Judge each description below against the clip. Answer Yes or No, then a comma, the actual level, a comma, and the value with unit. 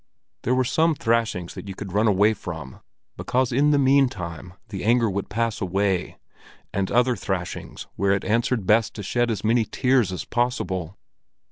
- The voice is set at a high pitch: No, low, 110 Hz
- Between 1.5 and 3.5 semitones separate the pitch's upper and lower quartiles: No, average, 4.3 semitones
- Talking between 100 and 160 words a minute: No, average, 170 wpm